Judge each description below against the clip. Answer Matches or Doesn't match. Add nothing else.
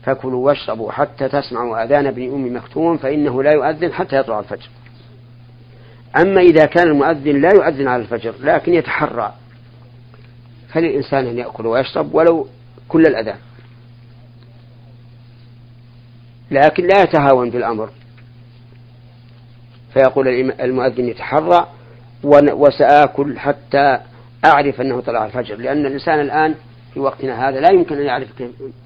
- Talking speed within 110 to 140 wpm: Matches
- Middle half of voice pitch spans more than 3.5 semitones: Doesn't match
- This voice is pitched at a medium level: Doesn't match